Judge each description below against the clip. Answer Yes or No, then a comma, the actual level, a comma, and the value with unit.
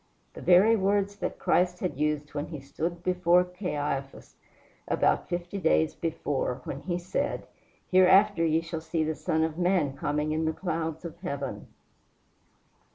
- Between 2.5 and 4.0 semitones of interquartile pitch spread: Yes, average, 3.0 semitones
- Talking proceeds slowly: No, average, 155 wpm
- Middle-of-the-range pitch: Yes, medium, 165 Hz